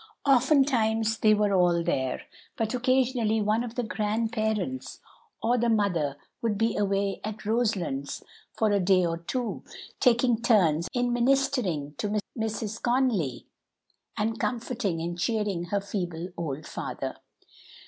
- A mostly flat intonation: No, average, 4.8 semitones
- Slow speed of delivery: Yes, slow, 130 wpm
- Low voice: No, high, 215 Hz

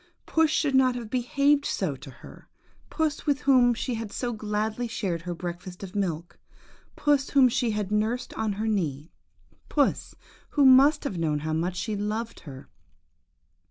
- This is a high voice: Yes, high, 220 Hz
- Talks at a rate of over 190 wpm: No, average, 165 wpm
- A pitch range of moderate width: No, wide, 6.5 semitones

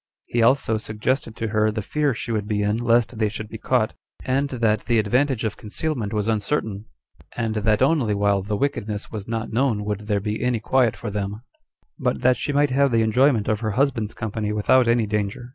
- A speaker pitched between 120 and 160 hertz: No, low, 110 Hz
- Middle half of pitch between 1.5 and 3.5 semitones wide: Yes, average, 2.9 semitones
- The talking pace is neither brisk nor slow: No, fast, 210 wpm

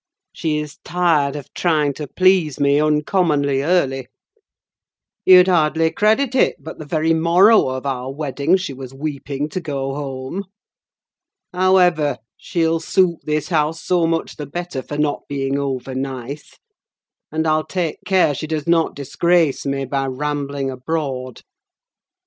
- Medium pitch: Yes, medium, 150 Hz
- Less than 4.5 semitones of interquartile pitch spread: Yes, average, 3.5 semitones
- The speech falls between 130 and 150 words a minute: Yes, average, 145 wpm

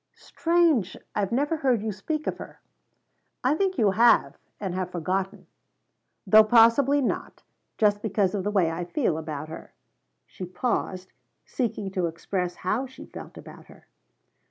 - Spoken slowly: No, average, 155 wpm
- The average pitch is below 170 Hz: No, high, 205 Hz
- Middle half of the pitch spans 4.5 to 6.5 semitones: Yes, wide, 5.5 semitones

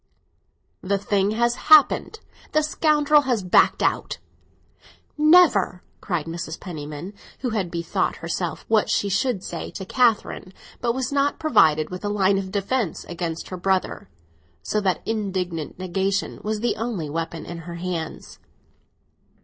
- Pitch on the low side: No, high, 195 Hz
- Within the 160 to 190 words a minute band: No, average, 140 wpm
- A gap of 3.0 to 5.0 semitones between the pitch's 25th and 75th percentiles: No, wide, 5.5 semitones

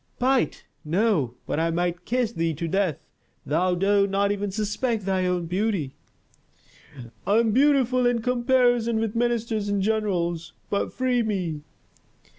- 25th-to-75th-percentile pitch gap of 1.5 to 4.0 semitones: No, average, 4.8 semitones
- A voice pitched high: Yes, high, 205 Hz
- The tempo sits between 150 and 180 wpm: No, average, 140 wpm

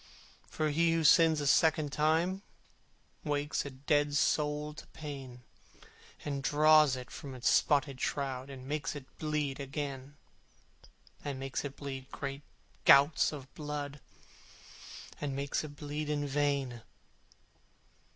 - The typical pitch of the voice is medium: Yes, medium, 145 Hz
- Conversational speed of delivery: No, slow, 130 wpm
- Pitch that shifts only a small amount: Yes, narrow, 1.7 semitones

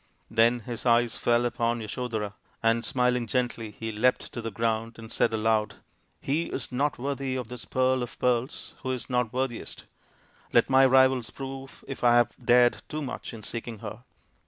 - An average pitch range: No, narrow, 2.2 semitones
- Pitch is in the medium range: No, low, 120 Hz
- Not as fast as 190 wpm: Yes, average, 180 wpm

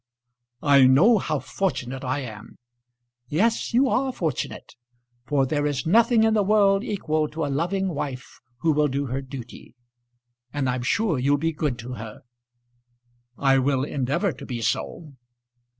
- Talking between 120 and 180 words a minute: Yes, average, 155 wpm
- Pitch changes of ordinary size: No, wide, 6.6 semitones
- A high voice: No, medium, 145 Hz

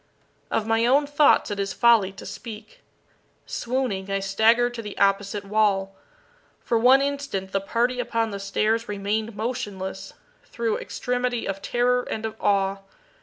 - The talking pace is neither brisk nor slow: Yes, average, 150 wpm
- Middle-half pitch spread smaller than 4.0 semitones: Yes, average, 3.5 semitones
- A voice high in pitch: Yes, high, 220 Hz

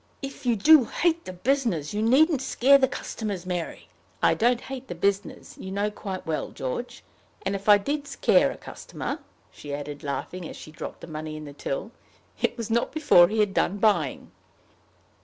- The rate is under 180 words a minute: No, average, 190 wpm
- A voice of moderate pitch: No, high, 205 Hz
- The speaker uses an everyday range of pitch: No, wide, 6.8 semitones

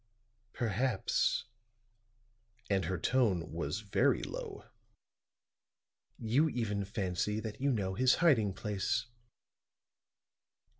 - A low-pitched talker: Yes, low, 105 Hz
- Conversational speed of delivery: No, slow, 90 wpm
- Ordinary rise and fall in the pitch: Yes, average, 4.2 semitones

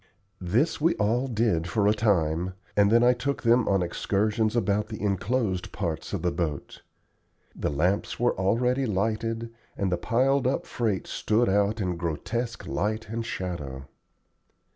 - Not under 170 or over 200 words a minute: No, average, 155 wpm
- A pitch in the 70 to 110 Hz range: Yes, low, 105 Hz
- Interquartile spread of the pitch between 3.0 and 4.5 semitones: Yes, average, 4.2 semitones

